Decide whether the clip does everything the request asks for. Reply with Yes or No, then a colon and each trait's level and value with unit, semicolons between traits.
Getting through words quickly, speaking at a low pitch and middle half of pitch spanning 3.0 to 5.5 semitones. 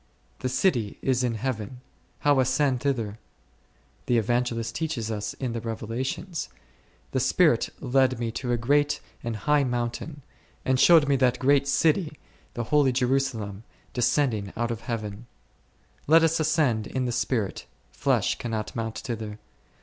No: average, 145 wpm; low, 125 Hz; average, 3.5 semitones